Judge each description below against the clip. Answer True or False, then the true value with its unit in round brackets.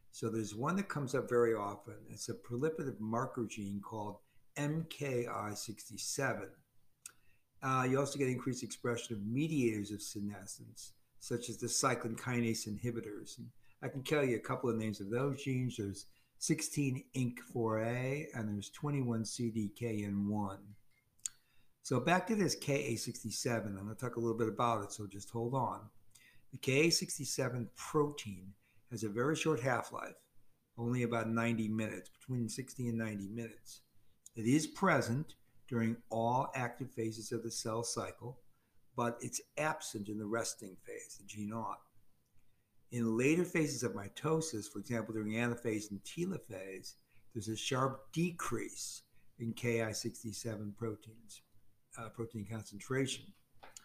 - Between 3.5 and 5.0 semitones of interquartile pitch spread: False (3.1 semitones)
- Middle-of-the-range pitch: False (115 Hz)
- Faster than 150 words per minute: False (140 wpm)